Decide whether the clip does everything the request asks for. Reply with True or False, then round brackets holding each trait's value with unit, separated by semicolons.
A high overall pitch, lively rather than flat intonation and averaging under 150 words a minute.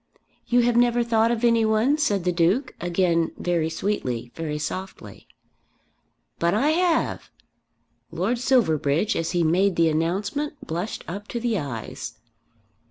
True (195 Hz; 6.2 semitones; 140 wpm)